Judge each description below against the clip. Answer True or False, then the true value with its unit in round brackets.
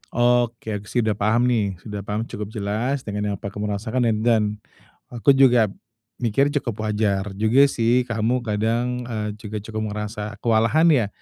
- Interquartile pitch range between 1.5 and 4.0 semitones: True (2.6 semitones)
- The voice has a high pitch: False (110 Hz)